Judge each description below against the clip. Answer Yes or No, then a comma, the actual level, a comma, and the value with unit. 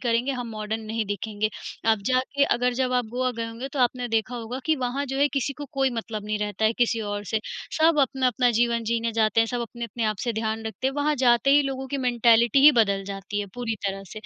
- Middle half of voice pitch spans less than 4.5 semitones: Yes, average, 2.7 semitones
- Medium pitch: No, high, 235 Hz